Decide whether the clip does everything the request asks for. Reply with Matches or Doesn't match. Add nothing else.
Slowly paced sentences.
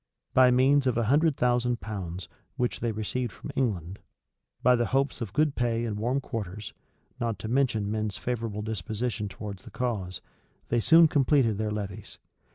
Doesn't match